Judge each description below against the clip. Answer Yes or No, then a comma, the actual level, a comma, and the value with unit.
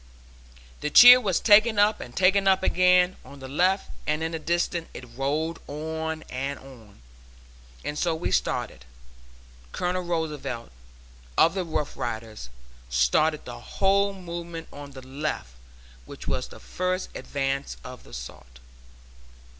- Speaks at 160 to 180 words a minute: No, average, 140 wpm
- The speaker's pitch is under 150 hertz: No, medium, 160 Hz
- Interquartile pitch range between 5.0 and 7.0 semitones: Yes, average, 5.3 semitones